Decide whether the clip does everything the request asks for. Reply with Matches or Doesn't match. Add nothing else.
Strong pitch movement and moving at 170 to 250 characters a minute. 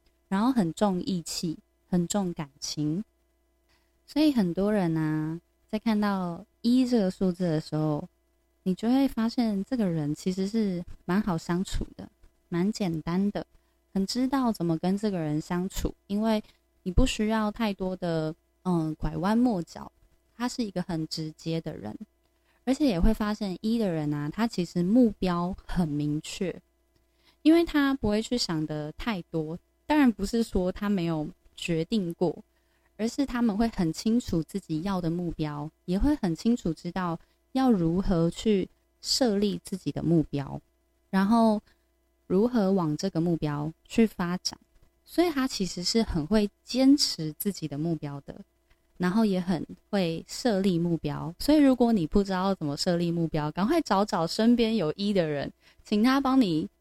Matches